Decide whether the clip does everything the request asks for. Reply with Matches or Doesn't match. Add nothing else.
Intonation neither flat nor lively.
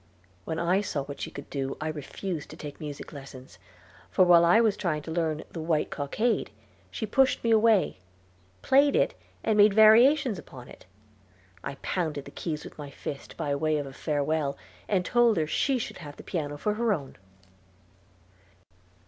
Doesn't match